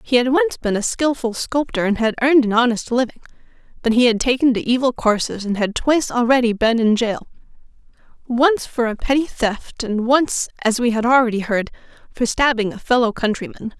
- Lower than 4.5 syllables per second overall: No, 5.4 syllables/s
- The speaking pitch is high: Yes, high, 240 Hz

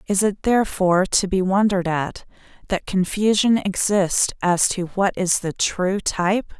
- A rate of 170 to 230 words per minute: No, average, 155 wpm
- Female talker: Yes, female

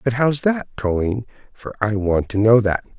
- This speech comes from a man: Yes, male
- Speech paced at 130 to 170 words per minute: No, average, 200 wpm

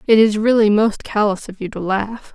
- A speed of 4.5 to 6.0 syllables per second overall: Yes, 5.0 syllables/s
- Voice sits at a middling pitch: No, high, 210 Hz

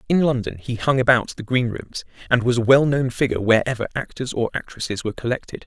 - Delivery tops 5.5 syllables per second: Yes, 6.2 syllables/s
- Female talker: No, male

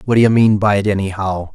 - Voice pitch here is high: No, low, 100 Hz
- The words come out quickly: Yes, fast, 235 wpm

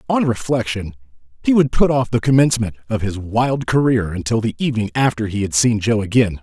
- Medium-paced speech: Yes, average, 195 wpm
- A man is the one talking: Yes, male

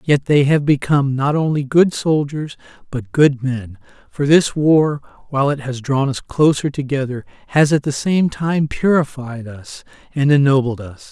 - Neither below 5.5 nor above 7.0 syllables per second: No, 4.5 syllables/s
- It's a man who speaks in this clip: Yes, male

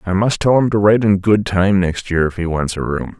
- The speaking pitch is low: Yes, very low, 95 Hz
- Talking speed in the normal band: No, fast, 300 wpm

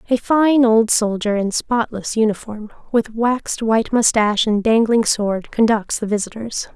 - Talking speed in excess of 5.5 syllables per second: No, 4.6 syllables/s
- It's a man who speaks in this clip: No, female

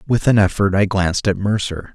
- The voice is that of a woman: No, male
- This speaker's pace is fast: Yes, fast, 215 wpm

